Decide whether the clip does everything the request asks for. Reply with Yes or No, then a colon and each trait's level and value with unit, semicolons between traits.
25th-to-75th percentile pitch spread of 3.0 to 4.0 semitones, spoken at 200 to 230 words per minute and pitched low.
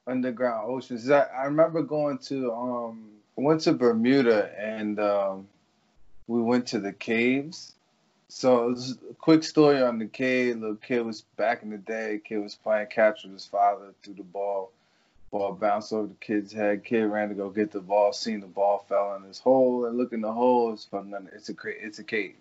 Yes: average, 3.6 semitones; fast, 205 wpm; low, 110 Hz